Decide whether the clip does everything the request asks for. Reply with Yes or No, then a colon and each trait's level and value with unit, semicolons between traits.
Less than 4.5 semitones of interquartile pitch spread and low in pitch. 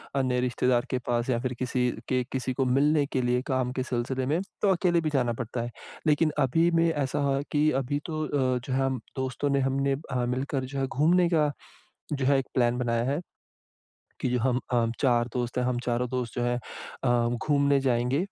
Yes: narrow, 2.4 semitones; low, 130 Hz